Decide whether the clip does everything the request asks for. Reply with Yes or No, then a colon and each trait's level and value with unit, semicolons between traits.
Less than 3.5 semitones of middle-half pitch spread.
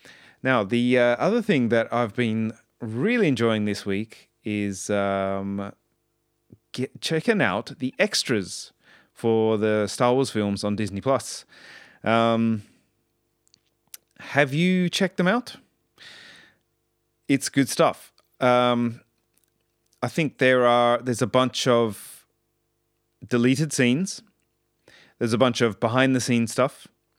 Yes: average, 2.9 semitones